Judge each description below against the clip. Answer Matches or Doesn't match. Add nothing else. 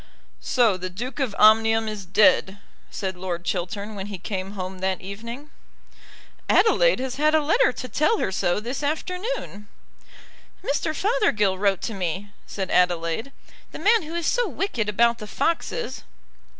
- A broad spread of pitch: Matches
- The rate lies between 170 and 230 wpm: Doesn't match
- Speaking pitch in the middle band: Doesn't match